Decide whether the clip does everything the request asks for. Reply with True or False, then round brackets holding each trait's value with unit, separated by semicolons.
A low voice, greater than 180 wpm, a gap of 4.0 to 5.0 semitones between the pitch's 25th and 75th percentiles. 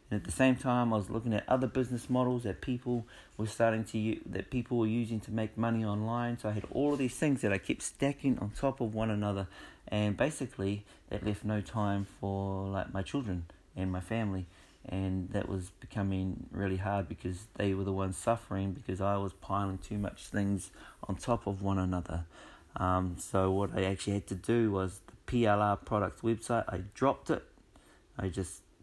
False (105 Hz; 200 wpm; 3.2 semitones)